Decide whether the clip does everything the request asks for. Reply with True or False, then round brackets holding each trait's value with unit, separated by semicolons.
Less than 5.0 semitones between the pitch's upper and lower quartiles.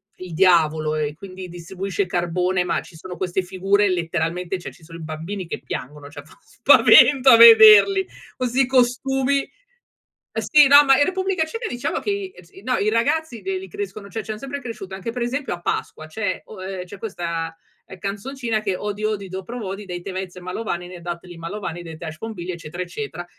False (5.4 semitones)